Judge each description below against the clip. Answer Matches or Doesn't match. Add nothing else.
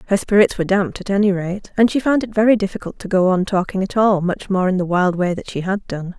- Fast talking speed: Matches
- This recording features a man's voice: Doesn't match